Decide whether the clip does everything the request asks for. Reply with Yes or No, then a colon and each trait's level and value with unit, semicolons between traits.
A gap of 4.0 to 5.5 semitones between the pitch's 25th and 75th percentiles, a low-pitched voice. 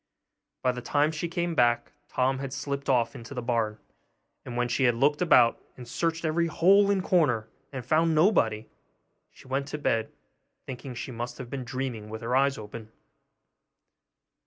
Yes: average, 4.3 semitones; low, 130 Hz